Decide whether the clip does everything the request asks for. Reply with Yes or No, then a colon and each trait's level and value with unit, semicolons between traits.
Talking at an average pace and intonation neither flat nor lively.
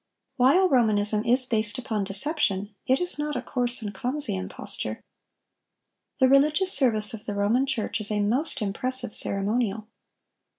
Yes: average, 145 wpm; average, 4.3 semitones